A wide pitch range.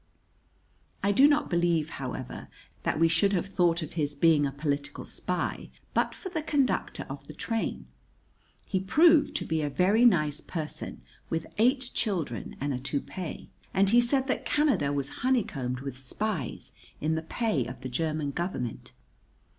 Yes: wide, 7.9 semitones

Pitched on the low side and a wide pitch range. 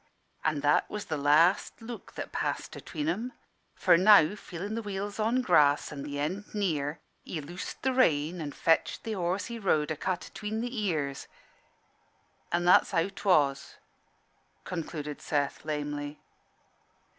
No: medium, 170 Hz; wide, 5.7 semitones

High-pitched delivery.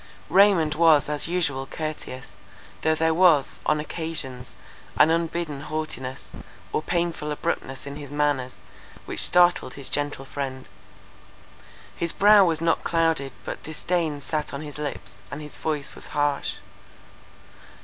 No: medium, 150 Hz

